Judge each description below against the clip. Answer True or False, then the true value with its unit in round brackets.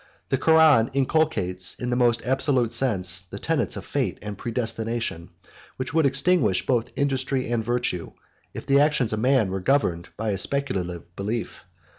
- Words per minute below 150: False (160 wpm)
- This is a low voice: True (120 Hz)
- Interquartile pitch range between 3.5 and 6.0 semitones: True (5.3 semitones)